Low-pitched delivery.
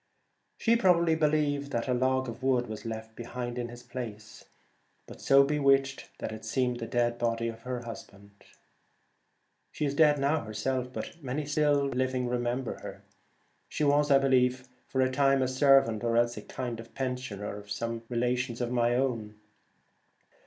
Yes: low, 125 Hz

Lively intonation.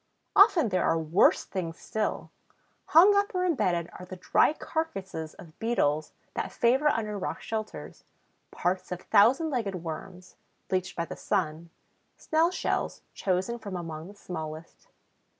Yes: wide, 5.9 semitones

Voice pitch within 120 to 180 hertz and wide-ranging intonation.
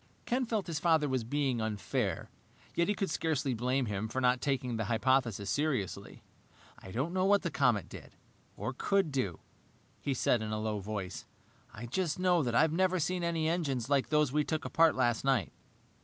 Yes: low, 135 Hz; wide, 6.0 semitones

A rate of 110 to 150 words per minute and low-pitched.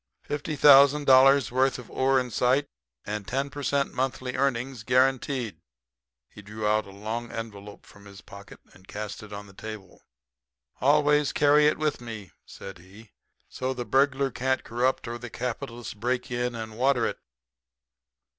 No: average, 165 wpm; low, 125 Hz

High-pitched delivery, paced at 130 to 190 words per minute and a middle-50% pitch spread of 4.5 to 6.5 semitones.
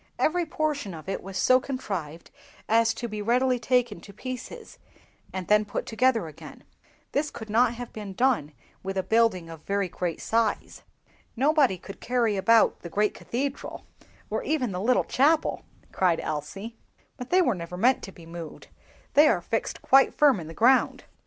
Yes: high, 225 Hz; average, 175 wpm; average, 5.2 semitones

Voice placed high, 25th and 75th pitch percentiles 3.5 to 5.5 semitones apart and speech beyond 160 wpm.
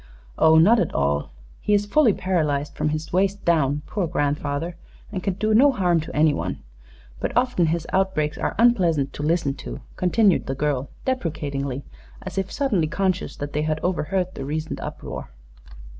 No: medium, 170 Hz; average, 4.6 semitones; average, 170 wpm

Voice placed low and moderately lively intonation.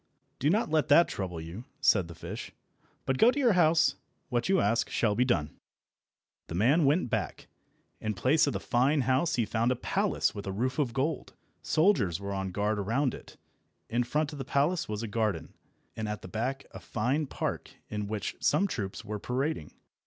No: low, 120 Hz; wide, 6.2 semitones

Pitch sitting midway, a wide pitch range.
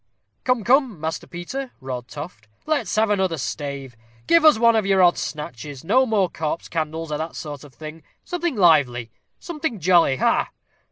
Yes: medium, 170 Hz; wide, 7.2 semitones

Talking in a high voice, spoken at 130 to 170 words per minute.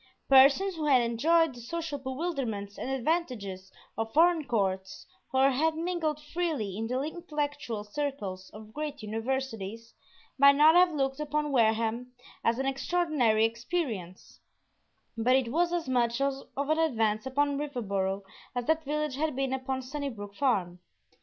Yes: very high, 265 Hz; average, 145 wpm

